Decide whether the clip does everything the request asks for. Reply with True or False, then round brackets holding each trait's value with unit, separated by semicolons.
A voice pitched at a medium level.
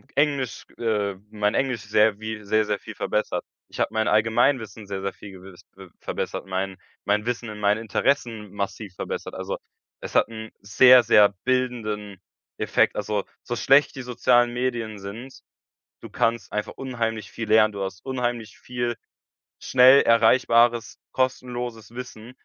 False (110 Hz)